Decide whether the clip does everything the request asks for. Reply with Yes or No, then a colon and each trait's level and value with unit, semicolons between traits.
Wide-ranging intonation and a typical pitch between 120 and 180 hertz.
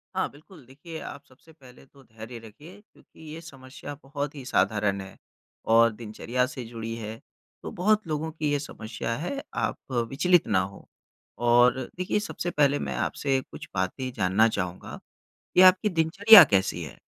Yes: wide, 6.1 semitones; low, 135 Hz